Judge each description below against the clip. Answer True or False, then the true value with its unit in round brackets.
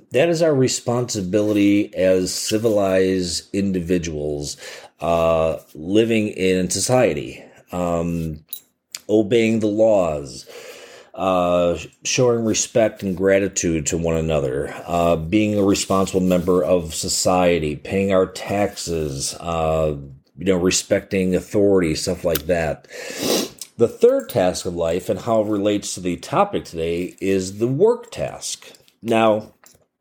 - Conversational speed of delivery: False (120 wpm)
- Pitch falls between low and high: False (95 Hz)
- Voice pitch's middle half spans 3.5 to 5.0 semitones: True (4.0 semitones)